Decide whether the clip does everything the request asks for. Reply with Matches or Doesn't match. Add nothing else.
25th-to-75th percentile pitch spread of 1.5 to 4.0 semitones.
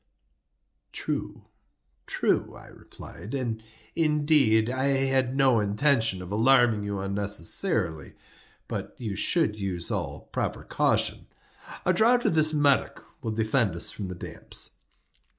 Doesn't match